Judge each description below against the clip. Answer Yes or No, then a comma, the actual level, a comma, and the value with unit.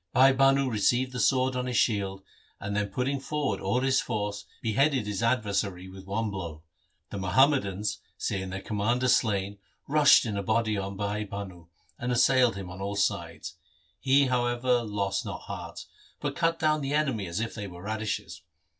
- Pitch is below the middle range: Yes, low, 110 Hz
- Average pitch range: Yes, average, 4.6 semitones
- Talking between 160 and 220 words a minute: Yes, average, 180 wpm